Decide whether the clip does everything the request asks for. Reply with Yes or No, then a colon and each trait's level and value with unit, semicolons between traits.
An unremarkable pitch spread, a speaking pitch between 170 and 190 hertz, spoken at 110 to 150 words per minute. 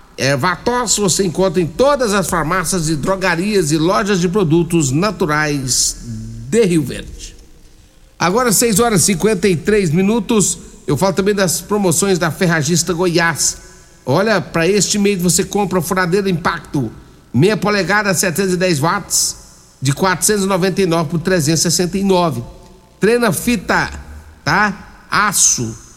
Yes: average, 3.3 semitones; medium, 185 Hz; average, 125 wpm